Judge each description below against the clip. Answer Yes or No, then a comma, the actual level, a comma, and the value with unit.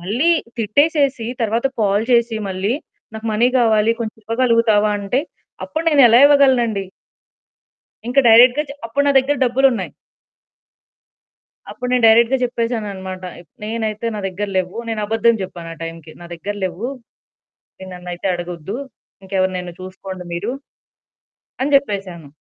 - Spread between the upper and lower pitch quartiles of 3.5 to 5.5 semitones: Yes, average, 4.5 semitones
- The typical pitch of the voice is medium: No, high, 220 Hz